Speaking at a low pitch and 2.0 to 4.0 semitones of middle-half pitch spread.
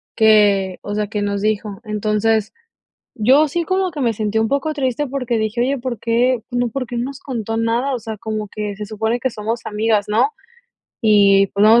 No: high, 225 Hz; average, 2.9 semitones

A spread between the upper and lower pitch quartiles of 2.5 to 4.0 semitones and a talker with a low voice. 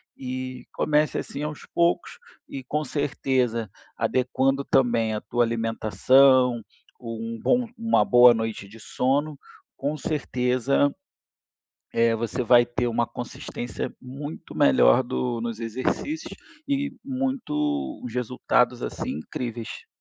Yes: average, 3.6 semitones; low, 125 Hz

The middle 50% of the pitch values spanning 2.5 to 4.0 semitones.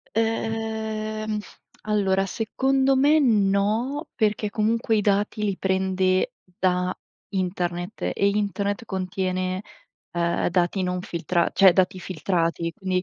Yes: average, 2.8 semitones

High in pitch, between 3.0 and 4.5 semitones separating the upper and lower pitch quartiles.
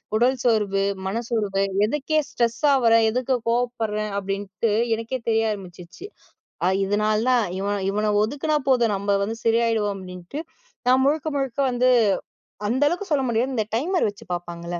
Yes: high, 225 Hz; average, 3.9 semitones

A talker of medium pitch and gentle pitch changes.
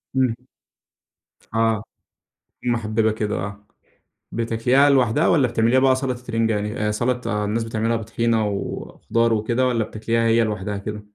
No: low, 115 Hz; narrow, 2.2 semitones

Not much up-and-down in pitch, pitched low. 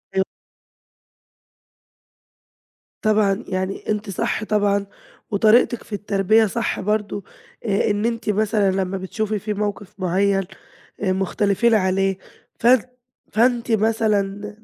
No: narrow, 1.8 semitones; high, 205 Hz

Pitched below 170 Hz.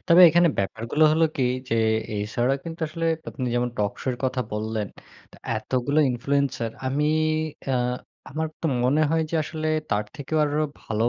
Yes: low, 135 Hz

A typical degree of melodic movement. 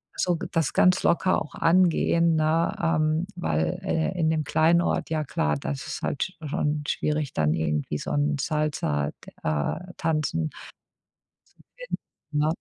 Yes: average, 3.0 semitones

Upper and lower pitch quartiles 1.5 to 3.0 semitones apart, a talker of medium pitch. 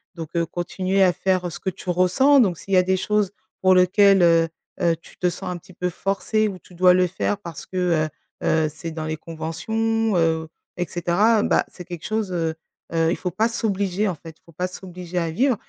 Yes: average, 2.7 semitones; medium, 180 Hz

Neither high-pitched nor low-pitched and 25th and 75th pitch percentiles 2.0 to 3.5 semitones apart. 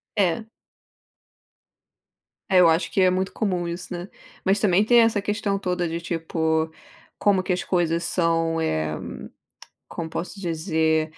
Yes: medium, 175 Hz; average, 2.9 semitones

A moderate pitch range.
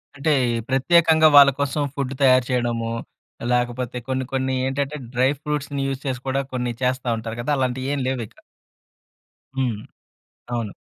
No: narrow, 2.2 semitones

